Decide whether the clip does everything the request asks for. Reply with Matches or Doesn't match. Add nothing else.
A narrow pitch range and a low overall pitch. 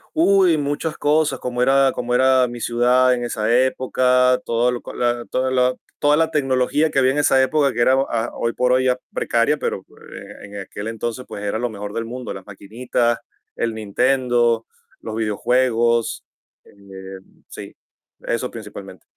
Matches